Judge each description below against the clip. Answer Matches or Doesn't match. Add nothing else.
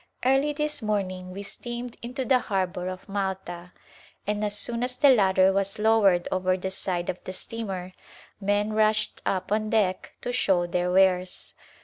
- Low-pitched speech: Doesn't match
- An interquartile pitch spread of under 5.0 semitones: Matches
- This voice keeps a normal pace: Matches